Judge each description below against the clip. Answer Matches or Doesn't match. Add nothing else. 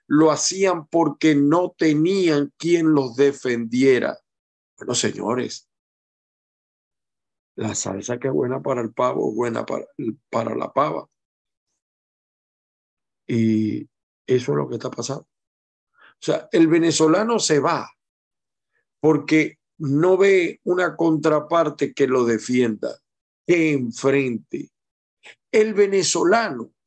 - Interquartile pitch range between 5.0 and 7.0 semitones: Matches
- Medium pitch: Matches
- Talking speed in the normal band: Doesn't match